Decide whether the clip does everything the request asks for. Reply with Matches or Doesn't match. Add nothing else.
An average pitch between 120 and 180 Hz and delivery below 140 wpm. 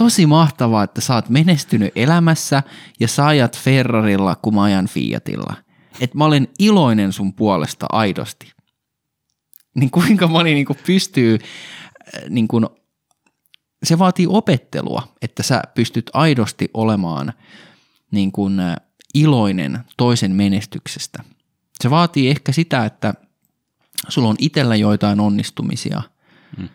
Matches